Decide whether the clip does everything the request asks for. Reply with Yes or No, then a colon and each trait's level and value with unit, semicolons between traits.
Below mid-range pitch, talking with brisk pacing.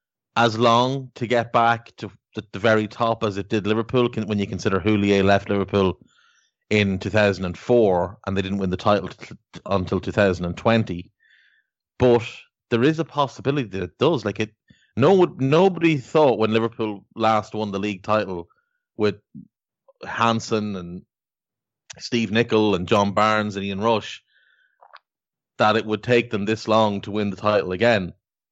No: low, 110 Hz; average, 160 wpm